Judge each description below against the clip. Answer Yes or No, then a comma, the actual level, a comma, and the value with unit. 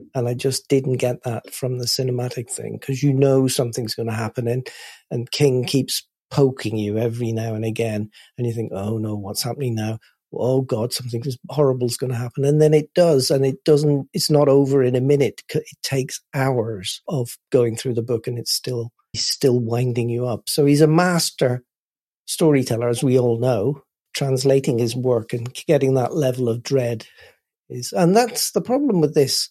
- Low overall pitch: Yes, low, 130 Hz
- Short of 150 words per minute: No, average, 195 wpm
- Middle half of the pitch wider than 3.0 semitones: No, average, 2.7 semitones